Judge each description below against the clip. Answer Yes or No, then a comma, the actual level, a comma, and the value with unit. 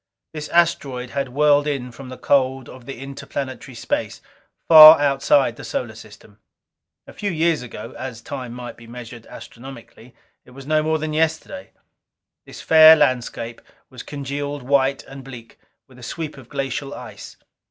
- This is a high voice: No, low, 135 Hz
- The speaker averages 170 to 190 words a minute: No, average, 160 wpm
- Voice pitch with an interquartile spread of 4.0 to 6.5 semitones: No, average, 3.1 semitones